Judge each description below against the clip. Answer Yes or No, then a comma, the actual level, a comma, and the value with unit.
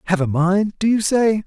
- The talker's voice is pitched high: Yes, high, 195 Hz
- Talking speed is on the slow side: No, fast, 245 wpm